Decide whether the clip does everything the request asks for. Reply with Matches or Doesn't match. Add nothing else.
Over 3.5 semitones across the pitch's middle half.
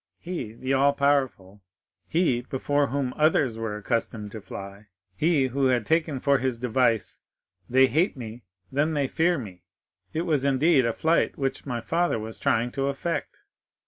Matches